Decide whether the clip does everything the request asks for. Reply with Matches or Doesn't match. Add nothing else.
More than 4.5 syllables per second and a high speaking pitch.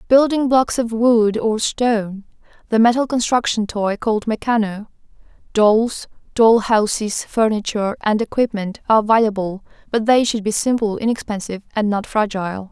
Matches